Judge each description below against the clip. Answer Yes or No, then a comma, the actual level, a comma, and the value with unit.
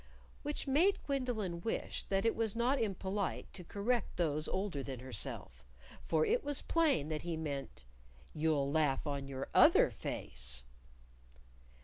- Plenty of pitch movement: Yes, wide, 8.2 semitones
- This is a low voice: No, medium, 170 Hz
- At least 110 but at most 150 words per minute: Yes, average, 140 wpm